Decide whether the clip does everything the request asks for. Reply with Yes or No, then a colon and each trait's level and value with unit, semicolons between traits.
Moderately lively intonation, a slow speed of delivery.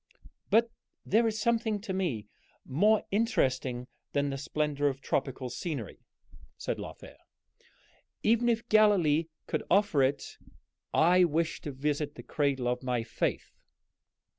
No: wide, 7.7 semitones; slow, 130 wpm